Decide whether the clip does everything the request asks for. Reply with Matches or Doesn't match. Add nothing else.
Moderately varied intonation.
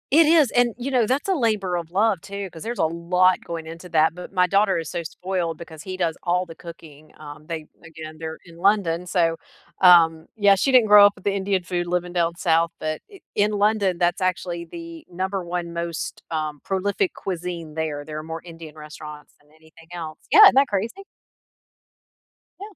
Matches